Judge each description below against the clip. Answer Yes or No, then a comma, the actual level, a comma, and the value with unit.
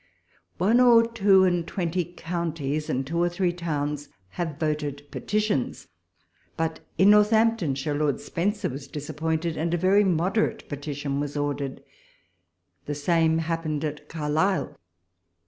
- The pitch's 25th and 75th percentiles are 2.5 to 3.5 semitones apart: No, average, 3.9 semitones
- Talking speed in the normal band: No, slow, 130 wpm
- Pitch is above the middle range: No, medium, 165 Hz